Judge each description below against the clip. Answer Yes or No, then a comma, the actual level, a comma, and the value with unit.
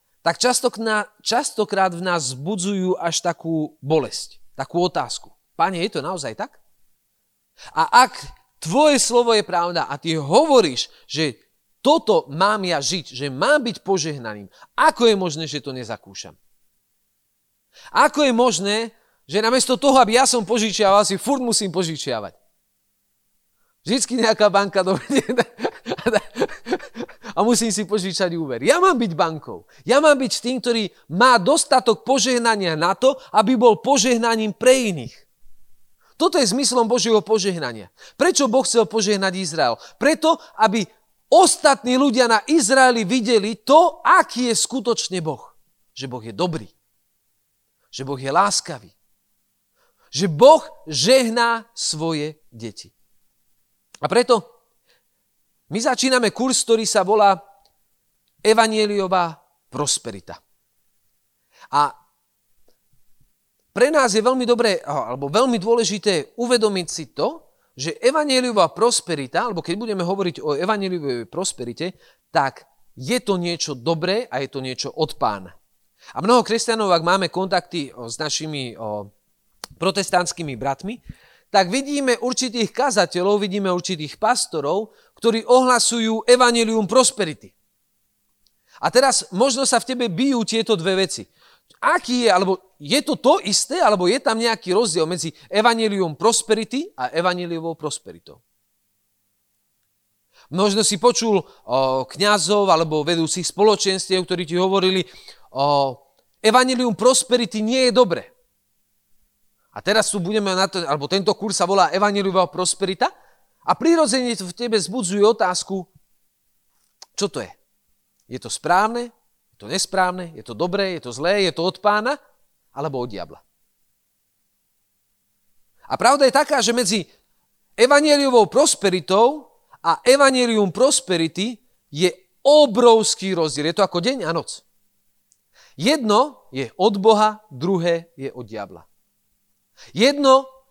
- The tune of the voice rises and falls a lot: Yes, wide, 7.0 semitones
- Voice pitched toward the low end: No, high, 200 Hz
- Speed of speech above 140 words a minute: No, average, 125 wpm